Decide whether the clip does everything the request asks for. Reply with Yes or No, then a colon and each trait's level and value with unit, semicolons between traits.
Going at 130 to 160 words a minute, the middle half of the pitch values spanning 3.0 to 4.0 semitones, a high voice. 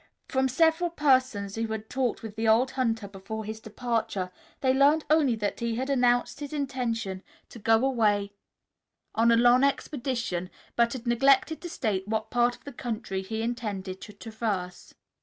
No: average, 170 wpm; average, 3.4 semitones; high, 235 Hz